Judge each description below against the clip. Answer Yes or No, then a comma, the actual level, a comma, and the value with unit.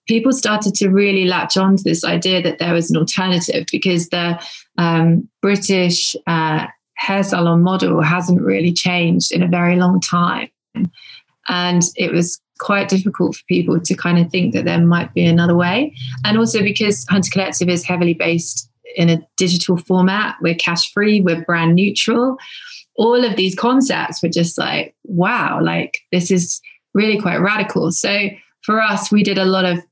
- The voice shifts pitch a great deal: No, average, 2.9 semitones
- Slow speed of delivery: No, average, 170 wpm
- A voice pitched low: No, medium, 180 Hz